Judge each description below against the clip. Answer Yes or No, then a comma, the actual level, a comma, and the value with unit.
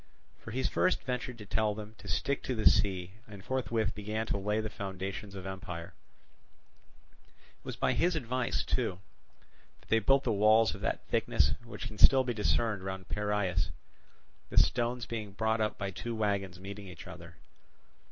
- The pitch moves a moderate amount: Yes, average, 3.1 semitones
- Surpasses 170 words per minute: Yes, average, 180 wpm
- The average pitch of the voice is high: No, low, 105 Hz